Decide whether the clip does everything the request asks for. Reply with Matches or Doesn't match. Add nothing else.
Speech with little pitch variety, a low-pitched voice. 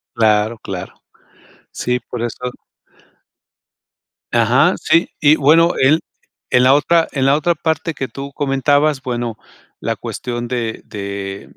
Doesn't match